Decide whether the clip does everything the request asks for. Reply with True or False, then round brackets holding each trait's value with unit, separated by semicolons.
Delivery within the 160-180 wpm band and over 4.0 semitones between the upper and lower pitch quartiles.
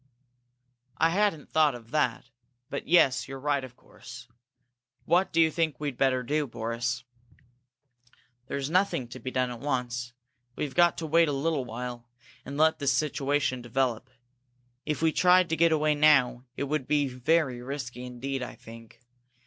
False (165 wpm; 3.7 semitones)